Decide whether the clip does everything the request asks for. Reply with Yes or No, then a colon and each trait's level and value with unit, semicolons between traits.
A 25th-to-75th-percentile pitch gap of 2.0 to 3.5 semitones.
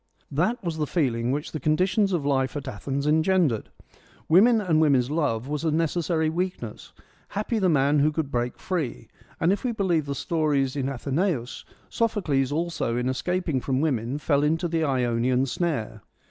No: average, 4.5 semitones